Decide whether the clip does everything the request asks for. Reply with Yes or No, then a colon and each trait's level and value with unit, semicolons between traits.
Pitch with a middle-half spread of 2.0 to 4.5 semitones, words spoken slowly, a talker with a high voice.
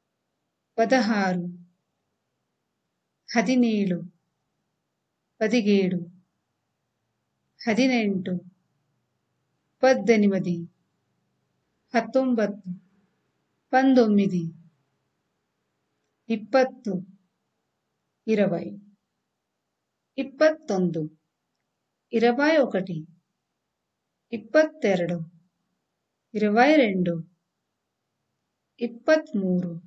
No: average, 4.9 semitones; slow, 30 wpm; high, 195 Hz